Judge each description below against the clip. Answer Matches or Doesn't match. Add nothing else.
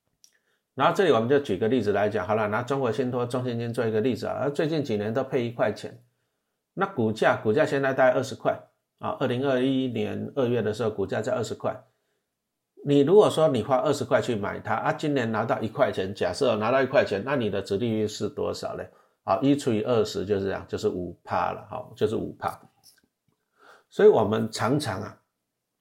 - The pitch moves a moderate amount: Matches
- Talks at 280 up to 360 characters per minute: Matches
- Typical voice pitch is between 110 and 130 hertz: Matches